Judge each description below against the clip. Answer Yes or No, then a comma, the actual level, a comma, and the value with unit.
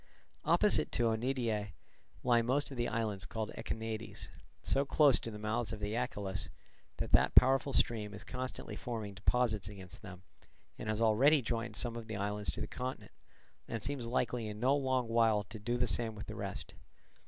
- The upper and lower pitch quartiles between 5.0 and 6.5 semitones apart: No, average, 2.7 semitones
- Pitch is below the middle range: Yes, low, 115 Hz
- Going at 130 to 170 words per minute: No, average, 185 wpm